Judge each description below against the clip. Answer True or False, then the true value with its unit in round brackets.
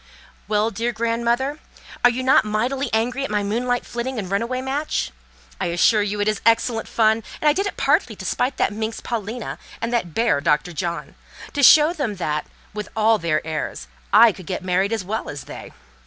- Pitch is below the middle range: False (225 Hz)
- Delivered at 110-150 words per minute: False (205 wpm)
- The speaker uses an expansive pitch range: False (3.7 semitones)